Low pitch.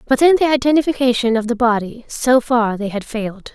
No: high, 240 Hz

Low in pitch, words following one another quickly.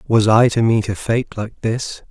Yes: low, 110 Hz; fast, 230 wpm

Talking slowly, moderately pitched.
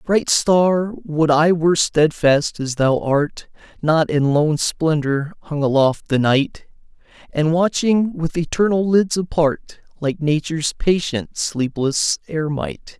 Yes: slow, 130 wpm; medium, 155 Hz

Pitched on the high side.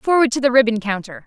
Yes: high, 245 Hz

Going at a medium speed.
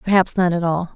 No: fast, 250 wpm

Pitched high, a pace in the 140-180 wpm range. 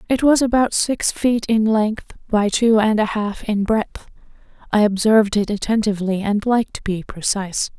Yes: high, 215 Hz; average, 175 wpm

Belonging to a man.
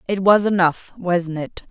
No: female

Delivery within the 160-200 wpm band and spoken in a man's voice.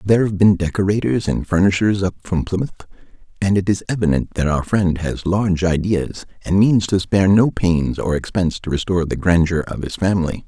Yes: average, 195 wpm; male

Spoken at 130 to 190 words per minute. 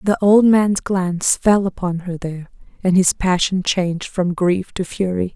Yes: average, 180 wpm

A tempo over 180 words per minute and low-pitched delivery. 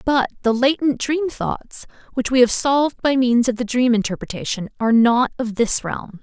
No: average, 195 wpm; high, 245 Hz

